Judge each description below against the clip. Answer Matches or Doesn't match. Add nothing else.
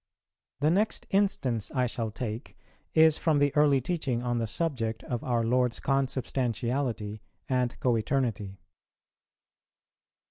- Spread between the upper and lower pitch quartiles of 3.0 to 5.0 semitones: Matches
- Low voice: Matches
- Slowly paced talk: Matches